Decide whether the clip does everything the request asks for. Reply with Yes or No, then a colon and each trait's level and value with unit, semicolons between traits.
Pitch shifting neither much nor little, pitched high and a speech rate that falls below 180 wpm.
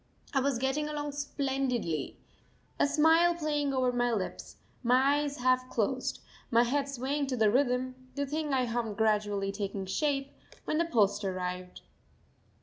Yes: average, 4.5 semitones; very high, 255 Hz; average, 150 wpm